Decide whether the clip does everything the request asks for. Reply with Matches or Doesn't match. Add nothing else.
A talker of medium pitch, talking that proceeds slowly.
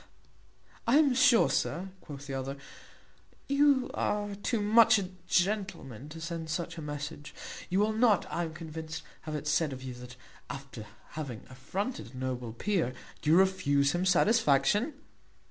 Doesn't match